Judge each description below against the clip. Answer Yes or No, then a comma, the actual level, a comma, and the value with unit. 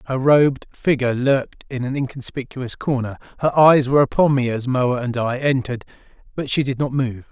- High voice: No, low, 130 Hz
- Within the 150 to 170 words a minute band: No, average, 190 wpm